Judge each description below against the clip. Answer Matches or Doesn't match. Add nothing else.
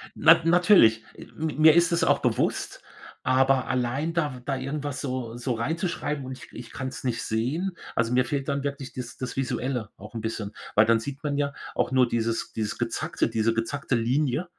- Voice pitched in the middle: Doesn't match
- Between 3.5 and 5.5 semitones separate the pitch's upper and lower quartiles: Matches